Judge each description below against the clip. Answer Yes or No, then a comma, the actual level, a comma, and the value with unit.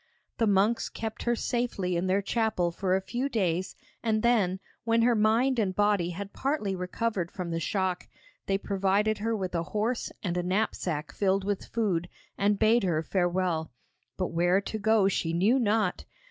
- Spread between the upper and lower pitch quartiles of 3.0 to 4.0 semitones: Yes, average, 3.5 semitones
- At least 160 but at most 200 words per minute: Yes, average, 175 wpm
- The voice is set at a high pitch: Yes, high, 200 Hz